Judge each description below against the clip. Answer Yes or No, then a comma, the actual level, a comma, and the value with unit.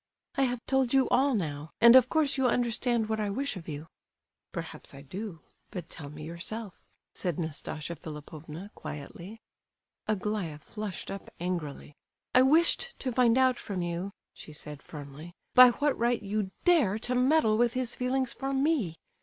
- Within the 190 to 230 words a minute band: No, average, 165 wpm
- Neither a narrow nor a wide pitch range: No, wide, 7.3 semitones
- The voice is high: Yes, high, 215 Hz